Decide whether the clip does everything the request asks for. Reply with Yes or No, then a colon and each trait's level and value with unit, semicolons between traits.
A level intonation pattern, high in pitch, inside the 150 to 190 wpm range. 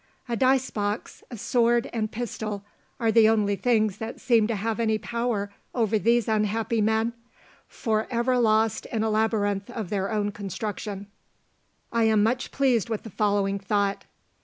Yes: narrow, 2.2 semitones; high, 220 Hz; average, 160 wpm